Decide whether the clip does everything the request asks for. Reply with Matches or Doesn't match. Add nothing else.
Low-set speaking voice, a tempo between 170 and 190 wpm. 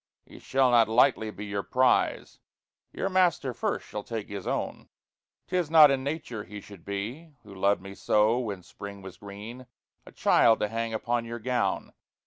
Matches